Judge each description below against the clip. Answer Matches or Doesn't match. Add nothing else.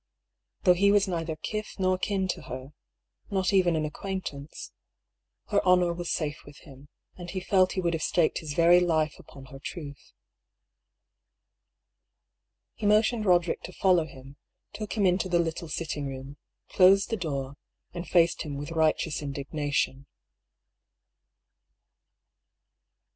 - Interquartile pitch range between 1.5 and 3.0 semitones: Doesn't match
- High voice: Doesn't match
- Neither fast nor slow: Matches